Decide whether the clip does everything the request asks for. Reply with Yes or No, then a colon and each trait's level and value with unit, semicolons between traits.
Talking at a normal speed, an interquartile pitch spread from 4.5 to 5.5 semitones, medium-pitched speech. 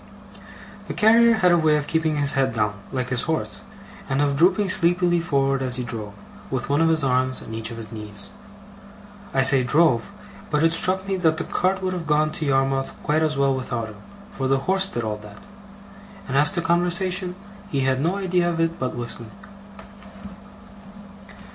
Yes: average, 190 wpm; average, 5.2 semitones; medium, 145 Hz